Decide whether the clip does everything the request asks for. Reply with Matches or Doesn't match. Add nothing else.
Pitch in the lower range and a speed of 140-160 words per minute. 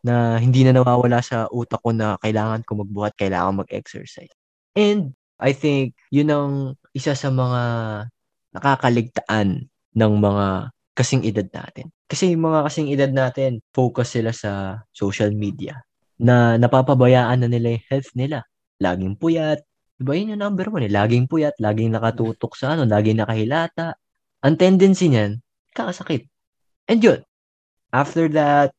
Matches